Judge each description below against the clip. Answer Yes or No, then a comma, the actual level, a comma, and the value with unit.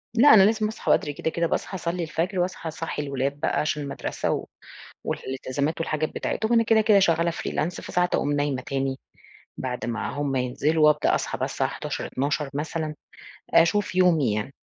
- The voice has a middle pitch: Yes, medium, 155 Hz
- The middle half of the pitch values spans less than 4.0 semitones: No, average, 4.3 semitones